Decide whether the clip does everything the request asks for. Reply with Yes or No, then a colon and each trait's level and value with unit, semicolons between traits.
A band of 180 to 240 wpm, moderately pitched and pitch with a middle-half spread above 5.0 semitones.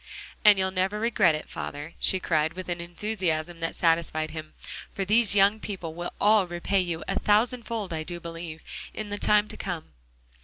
No: average, 190 wpm; medium, 180 Hz; average, 3.9 semitones